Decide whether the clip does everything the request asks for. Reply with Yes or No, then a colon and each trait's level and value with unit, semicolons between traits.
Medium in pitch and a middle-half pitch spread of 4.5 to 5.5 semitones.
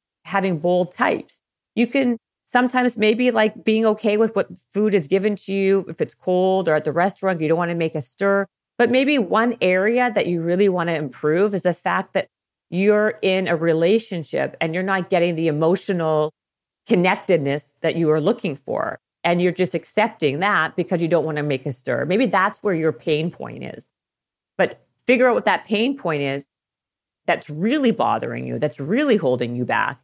Yes: medium, 180 Hz; average, 5.1 semitones